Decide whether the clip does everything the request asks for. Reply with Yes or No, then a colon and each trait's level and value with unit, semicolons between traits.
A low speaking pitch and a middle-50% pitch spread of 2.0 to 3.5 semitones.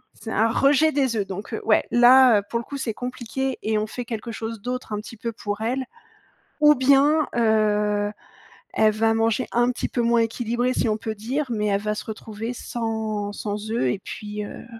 No: high, 225 Hz; average, 2.7 semitones